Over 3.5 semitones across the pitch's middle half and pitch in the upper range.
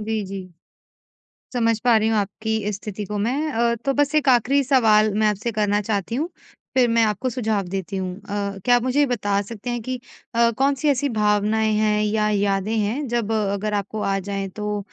No: average, 2.9 semitones; high, 215 Hz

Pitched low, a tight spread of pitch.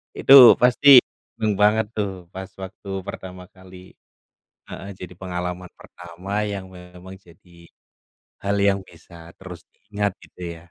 Yes: very low, 95 Hz; narrow, 2.2 semitones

